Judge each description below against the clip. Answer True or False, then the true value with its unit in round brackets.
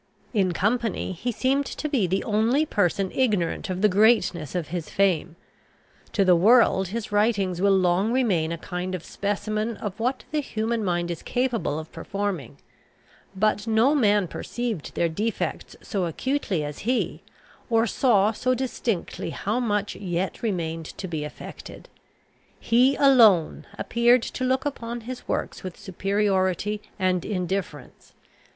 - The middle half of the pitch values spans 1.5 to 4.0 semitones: False (4.4 semitones)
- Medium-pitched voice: False (205 Hz)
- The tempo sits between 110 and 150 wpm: True (145 wpm)